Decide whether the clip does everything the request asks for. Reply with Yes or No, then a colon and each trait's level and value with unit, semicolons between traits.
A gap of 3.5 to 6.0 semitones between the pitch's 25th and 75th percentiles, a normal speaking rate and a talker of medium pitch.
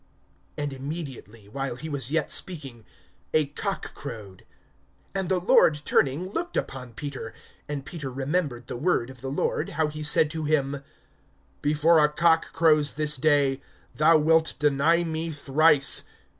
No: average, 3.1 semitones; average, 150 wpm; medium, 150 Hz